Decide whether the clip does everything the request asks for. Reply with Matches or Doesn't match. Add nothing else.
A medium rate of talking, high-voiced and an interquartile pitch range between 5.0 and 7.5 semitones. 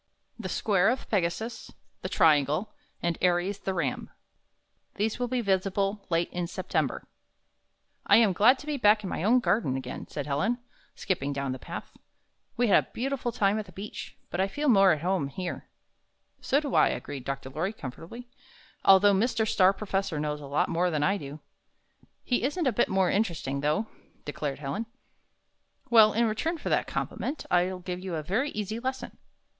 Matches